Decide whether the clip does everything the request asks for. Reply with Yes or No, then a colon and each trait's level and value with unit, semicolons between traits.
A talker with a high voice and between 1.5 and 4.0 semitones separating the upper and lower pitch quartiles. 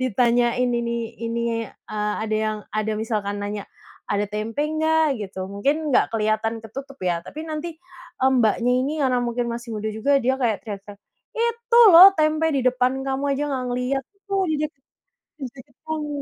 No: very high, 250 Hz; average, 4.9 semitones